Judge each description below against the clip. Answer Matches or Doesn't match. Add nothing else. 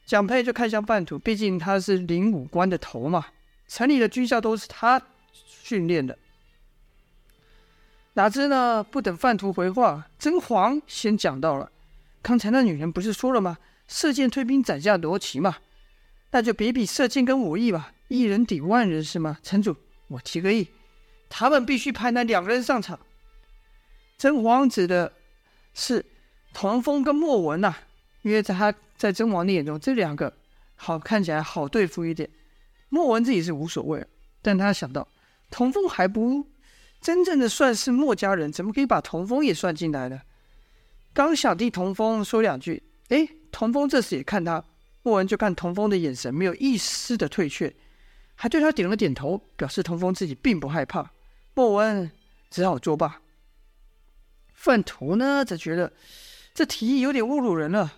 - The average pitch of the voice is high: Matches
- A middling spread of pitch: Doesn't match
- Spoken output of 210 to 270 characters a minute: Matches